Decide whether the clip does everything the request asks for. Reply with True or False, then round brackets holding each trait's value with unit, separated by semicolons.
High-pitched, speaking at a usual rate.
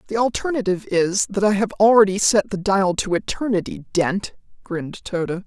True (200 Hz; 165 wpm)